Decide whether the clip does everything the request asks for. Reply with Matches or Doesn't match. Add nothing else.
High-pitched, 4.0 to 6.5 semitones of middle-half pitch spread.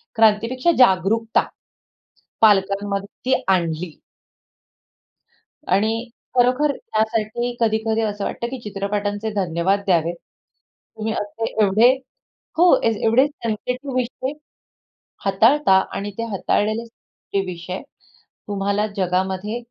Doesn't match